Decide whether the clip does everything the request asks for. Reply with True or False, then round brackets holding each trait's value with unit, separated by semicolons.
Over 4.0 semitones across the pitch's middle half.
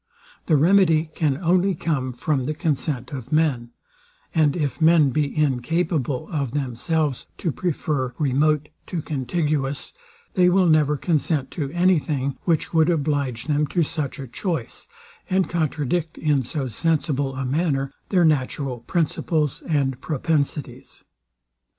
False (3.3 semitones)